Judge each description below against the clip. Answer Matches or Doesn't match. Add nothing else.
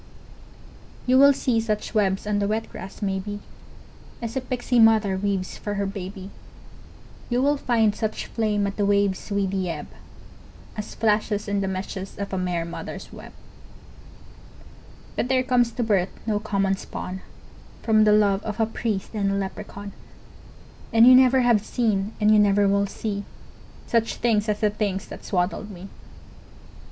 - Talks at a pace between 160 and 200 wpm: Matches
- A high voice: Matches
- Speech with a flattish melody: Matches